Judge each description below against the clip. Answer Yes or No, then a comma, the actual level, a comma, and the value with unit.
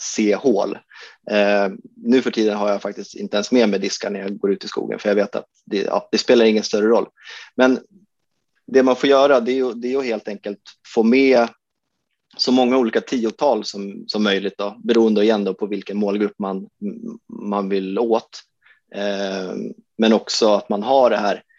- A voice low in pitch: Yes, low, 110 Hz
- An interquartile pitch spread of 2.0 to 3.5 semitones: No, average, 4.2 semitones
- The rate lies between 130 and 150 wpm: No, average, 190 wpm